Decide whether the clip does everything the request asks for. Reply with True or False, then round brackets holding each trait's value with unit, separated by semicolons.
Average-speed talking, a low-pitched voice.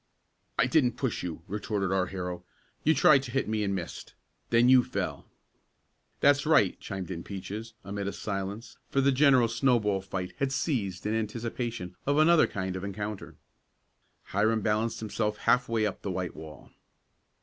True (170 wpm; 105 Hz)